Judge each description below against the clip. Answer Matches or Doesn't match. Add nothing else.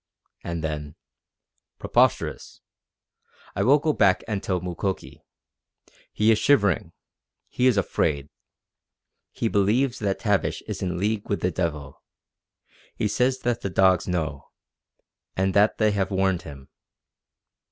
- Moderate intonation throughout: Matches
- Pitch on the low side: Matches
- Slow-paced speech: Matches